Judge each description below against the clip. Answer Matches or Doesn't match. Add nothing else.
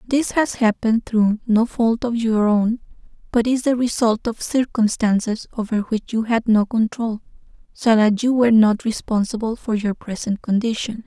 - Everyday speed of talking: Matches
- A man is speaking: Doesn't match